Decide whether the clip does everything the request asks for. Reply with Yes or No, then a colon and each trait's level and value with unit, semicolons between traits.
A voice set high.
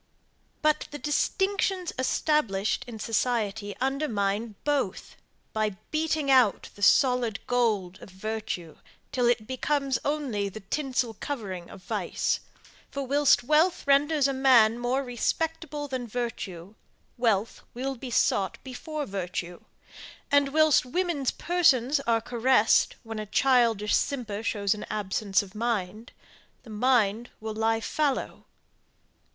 Yes: high, 240 Hz